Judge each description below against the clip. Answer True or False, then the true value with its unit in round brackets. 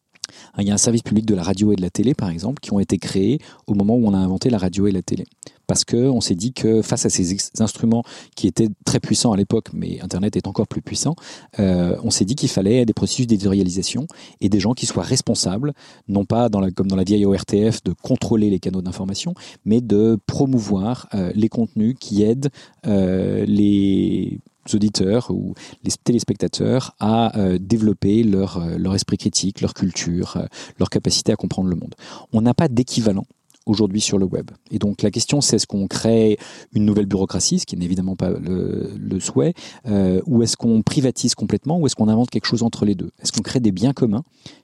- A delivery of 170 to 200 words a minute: False (215 wpm)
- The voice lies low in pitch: True (105 Hz)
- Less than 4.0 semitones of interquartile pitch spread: True (3.1 semitones)